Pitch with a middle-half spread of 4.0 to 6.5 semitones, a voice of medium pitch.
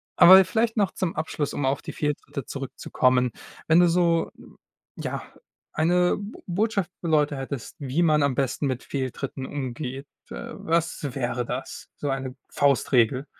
Yes: average, 4.4 semitones; medium, 145 Hz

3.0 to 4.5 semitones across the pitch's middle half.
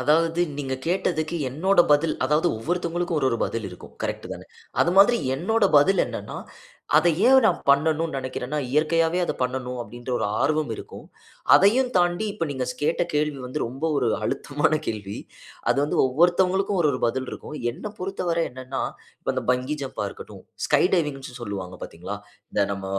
No: average, 5.1 semitones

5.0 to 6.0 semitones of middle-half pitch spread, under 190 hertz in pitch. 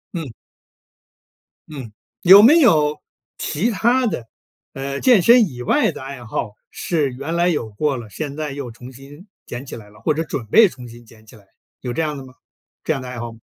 Yes: average, 5.3 semitones; medium, 140 Hz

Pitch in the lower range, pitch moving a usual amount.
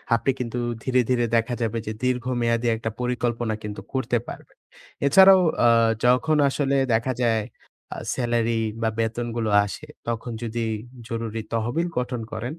No: low, 120 Hz; narrow, 1.8 semitones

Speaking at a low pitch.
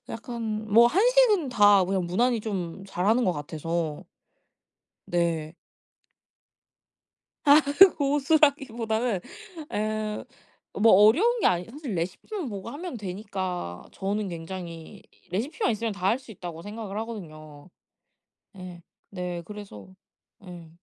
No: high, 205 Hz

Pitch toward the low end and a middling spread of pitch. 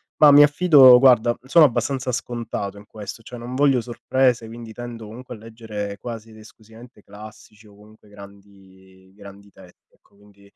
Yes: low, 110 Hz; average, 3.2 semitones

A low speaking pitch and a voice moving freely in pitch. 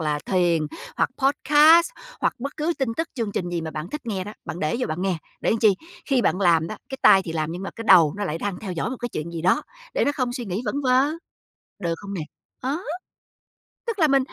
No: high, 200 Hz; wide, 7.4 semitones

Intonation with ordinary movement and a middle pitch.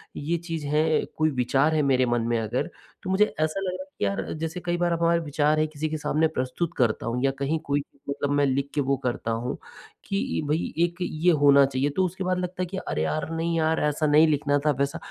Yes: average, 3.4 semitones; medium, 150 Hz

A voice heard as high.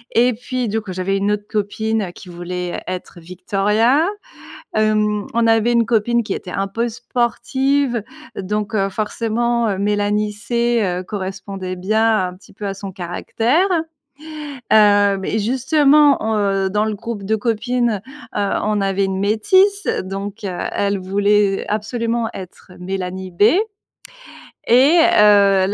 Yes: high, 210 Hz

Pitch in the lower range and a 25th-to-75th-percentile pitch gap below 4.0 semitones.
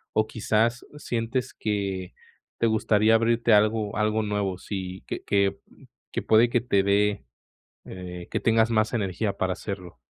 Yes: low, 105 Hz; narrow, 2.4 semitones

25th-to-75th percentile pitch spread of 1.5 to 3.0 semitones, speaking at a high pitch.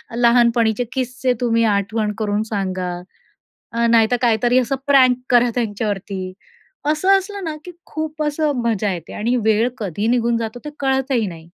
No: average, 3.4 semitones; high, 235 Hz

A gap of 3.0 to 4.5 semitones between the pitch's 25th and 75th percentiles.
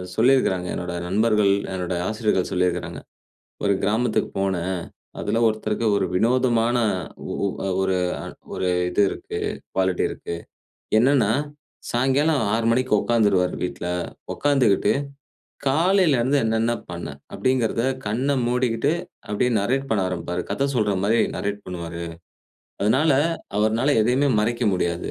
No: average, 5.0 semitones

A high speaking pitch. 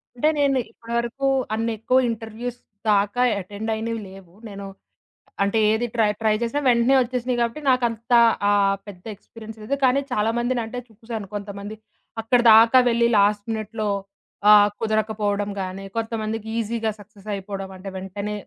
Yes: high, 220 Hz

